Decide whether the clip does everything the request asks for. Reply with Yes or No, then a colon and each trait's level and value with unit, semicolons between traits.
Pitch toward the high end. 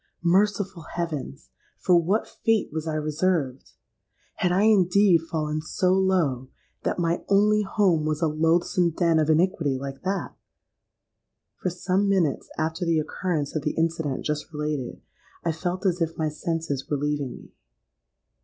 No: medium, 165 Hz